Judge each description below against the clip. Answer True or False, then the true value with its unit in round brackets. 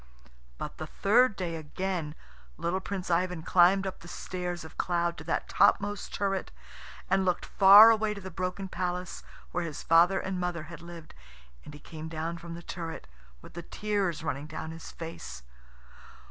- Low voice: False (175 Hz)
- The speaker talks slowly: False (175 wpm)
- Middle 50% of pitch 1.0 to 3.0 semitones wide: True (2.6 semitones)